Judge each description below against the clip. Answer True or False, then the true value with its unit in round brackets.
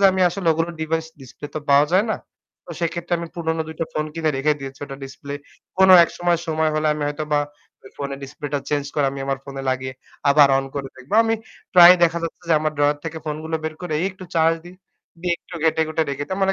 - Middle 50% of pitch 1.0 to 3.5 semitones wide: True (2.9 semitones)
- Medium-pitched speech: True (155 Hz)